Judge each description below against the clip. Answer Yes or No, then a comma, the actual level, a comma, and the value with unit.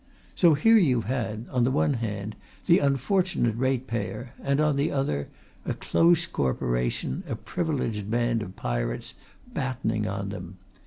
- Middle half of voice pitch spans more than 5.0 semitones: Yes, wide, 5.6 semitones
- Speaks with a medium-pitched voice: No, low, 120 Hz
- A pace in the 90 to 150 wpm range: Yes, average, 145 wpm